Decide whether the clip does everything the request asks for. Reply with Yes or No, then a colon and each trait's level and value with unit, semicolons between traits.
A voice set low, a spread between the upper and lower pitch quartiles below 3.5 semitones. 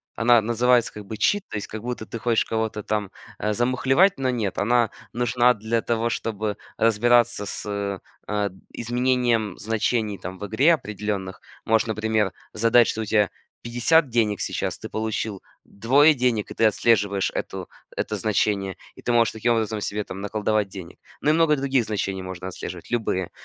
Yes: low, 110 Hz; average, 2.7 semitones